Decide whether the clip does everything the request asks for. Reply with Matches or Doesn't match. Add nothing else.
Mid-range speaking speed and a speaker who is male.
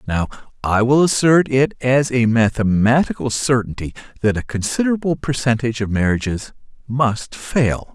Doesn't match